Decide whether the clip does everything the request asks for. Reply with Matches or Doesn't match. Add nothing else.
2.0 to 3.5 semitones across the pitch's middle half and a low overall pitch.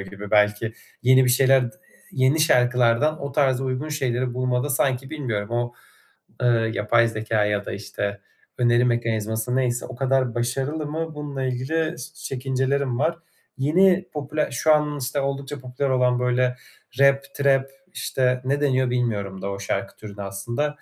Matches